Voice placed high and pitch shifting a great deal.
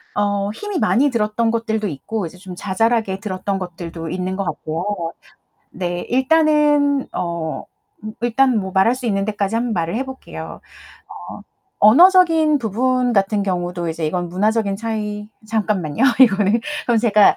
No: high, 210 Hz; average, 4.4 semitones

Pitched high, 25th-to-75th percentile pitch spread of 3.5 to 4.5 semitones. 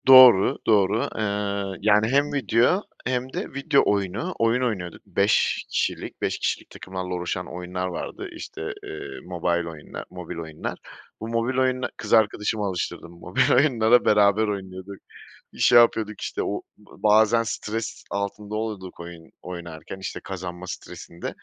No: low, 100 Hz; average, 3.9 semitones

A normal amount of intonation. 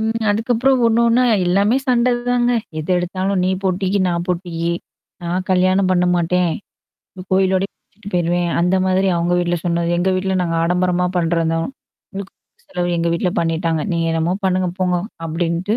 No: narrow, 2.2 semitones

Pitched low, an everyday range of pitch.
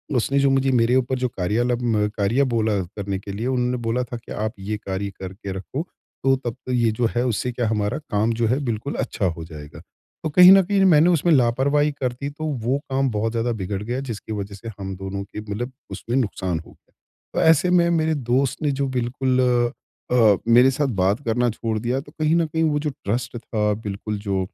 Yes: low, 120 Hz; average, 4.2 semitones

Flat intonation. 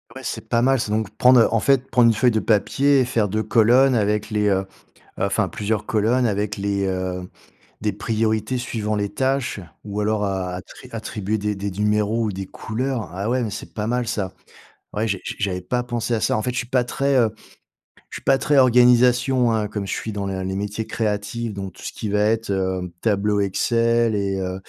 No: average, 3.0 semitones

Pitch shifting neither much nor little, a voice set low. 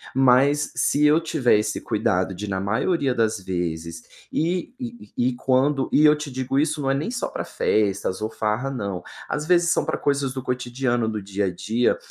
No: wide, 5.8 semitones; low, 125 Hz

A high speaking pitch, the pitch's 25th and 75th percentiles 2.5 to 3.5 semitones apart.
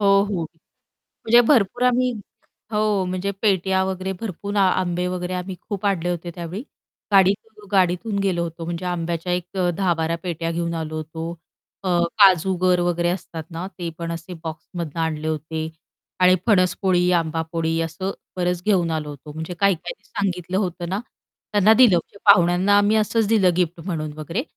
No: medium, 180 Hz; average, 2.9 semitones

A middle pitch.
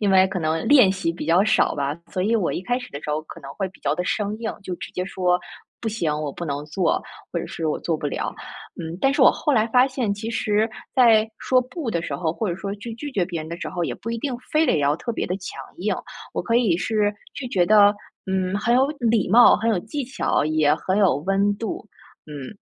No: high, 200 Hz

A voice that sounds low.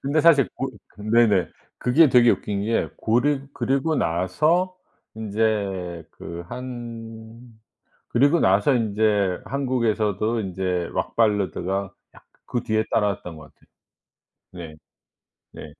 Yes: low, 110 Hz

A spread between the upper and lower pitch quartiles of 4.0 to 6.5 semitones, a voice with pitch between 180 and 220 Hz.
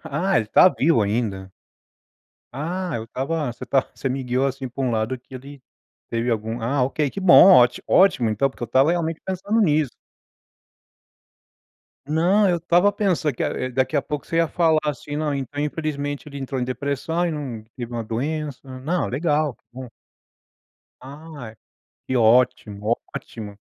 No: average, 4.6 semitones; medium, 140 Hz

